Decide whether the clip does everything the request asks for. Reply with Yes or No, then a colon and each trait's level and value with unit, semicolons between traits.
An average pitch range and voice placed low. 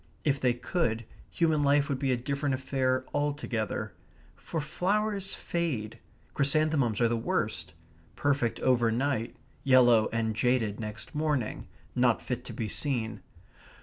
Yes: average, 3.9 semitones; low, 130 Hz